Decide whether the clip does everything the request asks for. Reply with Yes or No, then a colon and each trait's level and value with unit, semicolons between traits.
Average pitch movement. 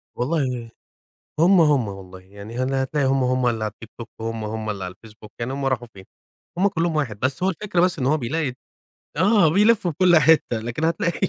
No: wide, 6.6 semitones